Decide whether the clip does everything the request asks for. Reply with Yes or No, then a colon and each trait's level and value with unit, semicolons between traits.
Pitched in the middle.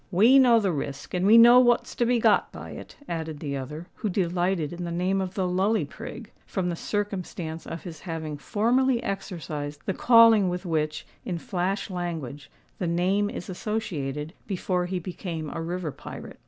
Yes: medium, 180 Hz